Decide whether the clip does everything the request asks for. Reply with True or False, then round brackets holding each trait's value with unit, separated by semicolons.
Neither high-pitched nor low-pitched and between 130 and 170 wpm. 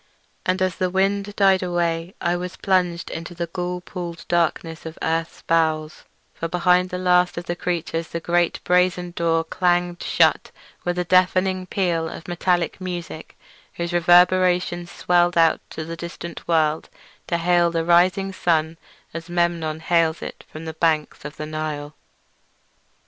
True (175 Hz; 155 wpm)